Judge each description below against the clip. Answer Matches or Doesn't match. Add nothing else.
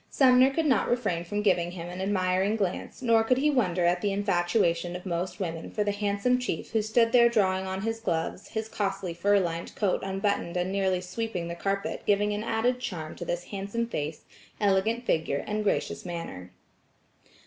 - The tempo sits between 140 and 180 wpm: Doesn't match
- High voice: Matches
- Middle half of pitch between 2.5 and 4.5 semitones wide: Matches